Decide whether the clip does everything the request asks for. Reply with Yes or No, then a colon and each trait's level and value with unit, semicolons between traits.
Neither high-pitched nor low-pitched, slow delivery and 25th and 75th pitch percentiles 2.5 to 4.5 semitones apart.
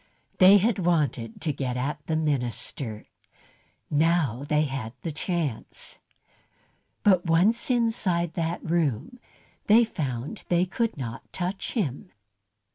No: medium, 160 Hz; slow, 120 wpm; wide, 5.5 semitones